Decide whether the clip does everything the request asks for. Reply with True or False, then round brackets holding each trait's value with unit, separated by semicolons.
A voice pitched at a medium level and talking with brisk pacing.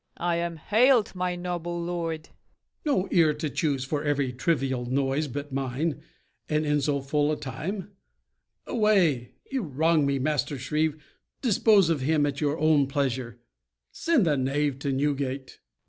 False (150 Hz; 160 wpm)